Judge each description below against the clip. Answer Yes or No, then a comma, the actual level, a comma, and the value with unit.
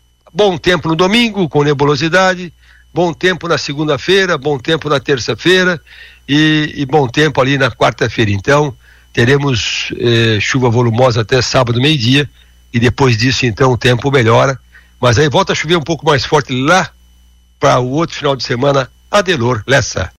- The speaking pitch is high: No, medium, 140 Hz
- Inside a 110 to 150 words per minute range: No, average, 160 wpm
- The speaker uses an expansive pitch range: No, average, 4.5 semitones